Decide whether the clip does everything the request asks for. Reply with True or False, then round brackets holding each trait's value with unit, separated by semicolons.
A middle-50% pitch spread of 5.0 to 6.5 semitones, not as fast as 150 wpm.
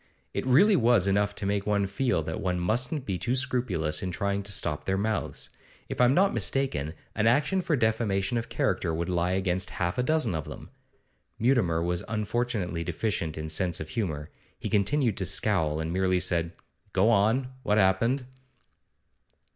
False (5.5 semitones; 175 wpm)